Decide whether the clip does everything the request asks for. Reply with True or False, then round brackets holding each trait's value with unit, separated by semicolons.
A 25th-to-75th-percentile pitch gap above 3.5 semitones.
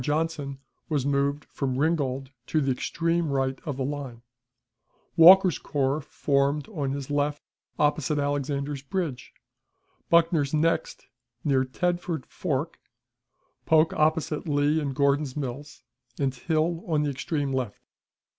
False (2.4 semitones)